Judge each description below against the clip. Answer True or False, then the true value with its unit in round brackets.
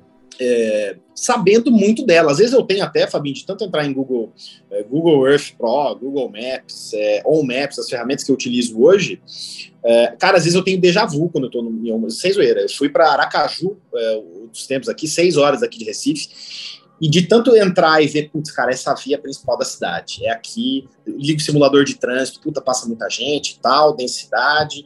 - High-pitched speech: False (150 Hz)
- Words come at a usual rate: False (205 wpm)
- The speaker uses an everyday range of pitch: False (6.9 semitones)